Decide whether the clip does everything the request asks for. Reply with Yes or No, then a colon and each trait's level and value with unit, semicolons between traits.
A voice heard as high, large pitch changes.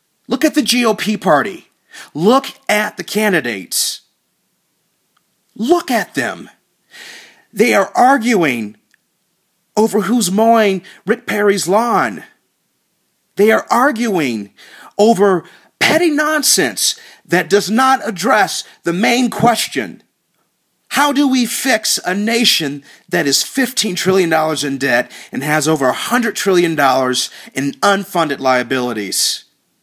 Yes: high, 205 Hz; wide, 7.1 semitones